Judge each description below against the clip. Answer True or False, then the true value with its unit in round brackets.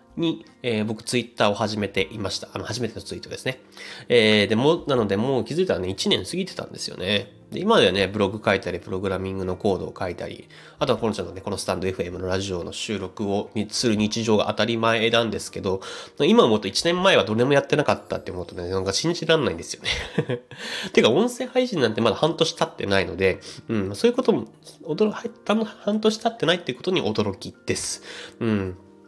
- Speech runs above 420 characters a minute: True (435 characters per minute)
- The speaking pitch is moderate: False (110 Hz)